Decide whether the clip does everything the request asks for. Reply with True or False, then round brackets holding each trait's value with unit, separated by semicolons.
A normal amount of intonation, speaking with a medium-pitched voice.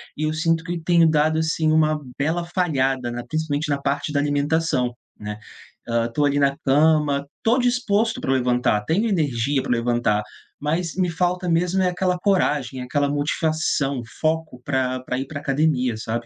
True (4.0 semitones; 150 Hz)